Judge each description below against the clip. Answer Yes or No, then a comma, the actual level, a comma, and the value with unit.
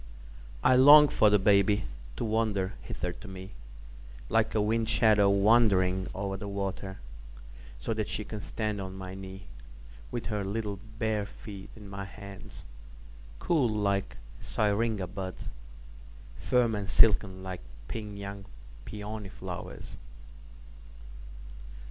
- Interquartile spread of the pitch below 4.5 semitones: Yes, narrow, 2.4 semitones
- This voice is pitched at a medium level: No, low, 100 Hz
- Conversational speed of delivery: No, slow, 110 wpm